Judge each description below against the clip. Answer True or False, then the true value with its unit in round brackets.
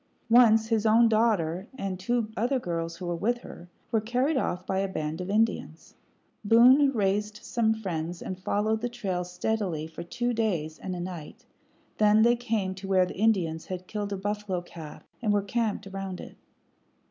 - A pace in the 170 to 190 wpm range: True (180 wpm)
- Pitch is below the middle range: False (205 Hz)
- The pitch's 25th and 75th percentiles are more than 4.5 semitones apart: False (3.8 semitones)